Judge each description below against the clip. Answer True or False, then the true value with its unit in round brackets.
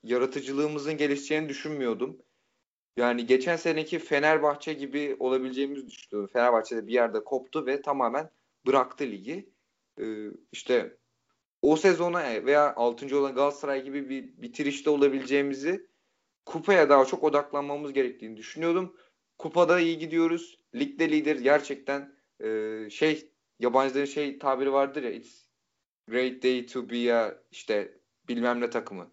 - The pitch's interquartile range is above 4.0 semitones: False (3.0 semitones)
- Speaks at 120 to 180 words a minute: True (125 wpm)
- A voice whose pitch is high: False (140 Hz)